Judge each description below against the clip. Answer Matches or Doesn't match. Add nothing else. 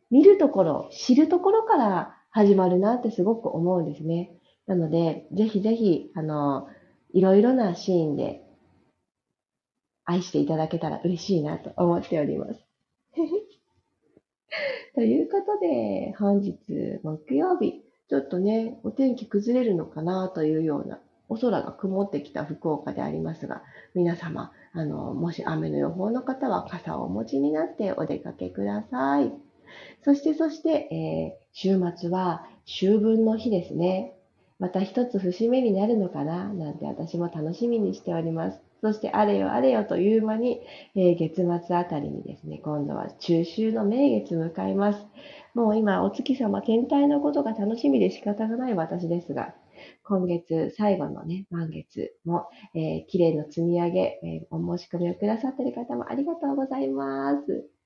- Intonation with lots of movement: Matches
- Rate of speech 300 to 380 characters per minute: Matches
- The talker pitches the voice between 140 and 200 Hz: Matches